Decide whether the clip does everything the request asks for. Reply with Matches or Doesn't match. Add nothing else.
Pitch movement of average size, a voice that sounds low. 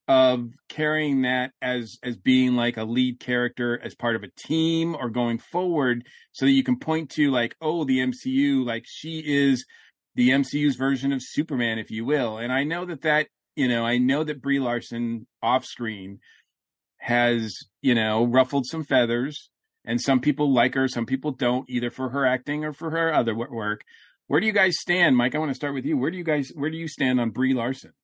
Matches